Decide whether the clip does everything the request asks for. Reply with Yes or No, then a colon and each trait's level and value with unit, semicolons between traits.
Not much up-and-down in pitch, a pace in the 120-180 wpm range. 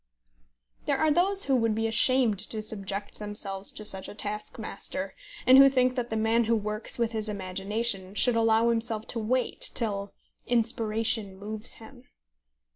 Yes: narrow, 2.3 semitones; average, 160 wpm